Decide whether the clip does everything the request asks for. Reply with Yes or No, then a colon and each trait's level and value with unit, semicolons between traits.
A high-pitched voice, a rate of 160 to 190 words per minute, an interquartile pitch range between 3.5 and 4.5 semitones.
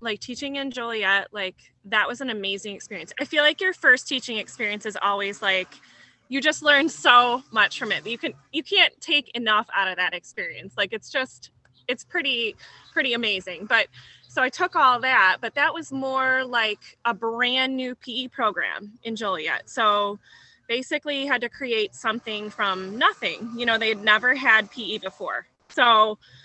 Yes: high, 235 Hz; average, 180 wpm; average, 4.1 semitones